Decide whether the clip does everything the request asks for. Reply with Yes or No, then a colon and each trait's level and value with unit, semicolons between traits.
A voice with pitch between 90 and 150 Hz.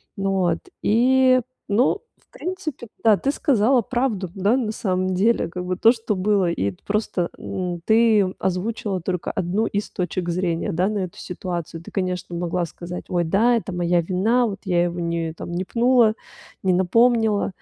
No: high, 190 Hz